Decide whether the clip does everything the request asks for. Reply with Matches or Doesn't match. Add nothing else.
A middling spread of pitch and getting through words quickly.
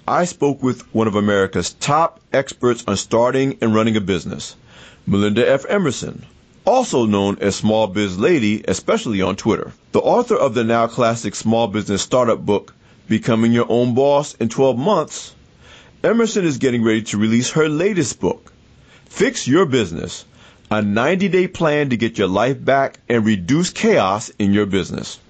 Doesn't match